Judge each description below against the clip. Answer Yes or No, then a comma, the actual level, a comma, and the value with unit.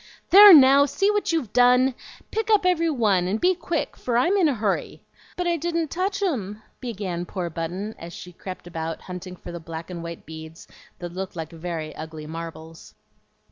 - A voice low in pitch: No, high, 200 Hz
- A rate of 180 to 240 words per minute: Yes, average, 190 wpm